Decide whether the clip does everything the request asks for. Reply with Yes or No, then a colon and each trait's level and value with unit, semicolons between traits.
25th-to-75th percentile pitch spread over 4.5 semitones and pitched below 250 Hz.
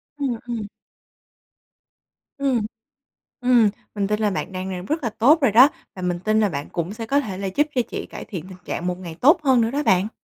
Yes: average, 5.3 semitones; high, 215 Hz